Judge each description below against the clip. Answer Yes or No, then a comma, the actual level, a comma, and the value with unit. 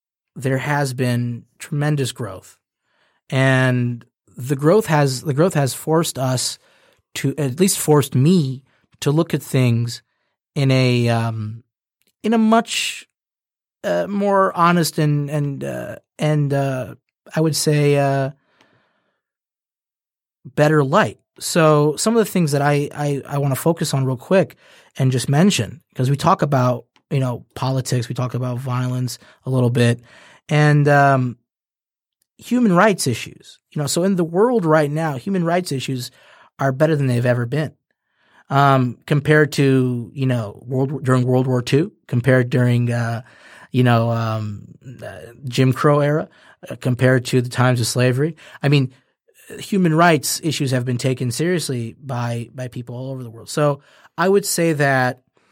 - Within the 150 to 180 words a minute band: Yes, average, 155 wpm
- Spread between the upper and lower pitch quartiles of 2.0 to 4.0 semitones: Yes, average, 3.4 semitones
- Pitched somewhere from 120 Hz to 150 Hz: Yes, low, 135 Hz